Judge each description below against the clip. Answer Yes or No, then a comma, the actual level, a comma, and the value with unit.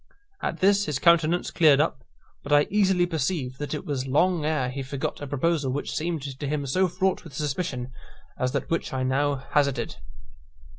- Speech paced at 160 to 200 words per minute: Yes, average, 190 wpm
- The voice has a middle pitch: Yes, medium, 145 Hz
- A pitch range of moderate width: Yes, average, 3.9 semitones